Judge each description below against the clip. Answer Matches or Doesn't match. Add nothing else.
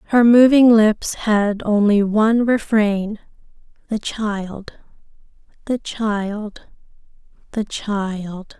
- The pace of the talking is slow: Matches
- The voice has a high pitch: Matches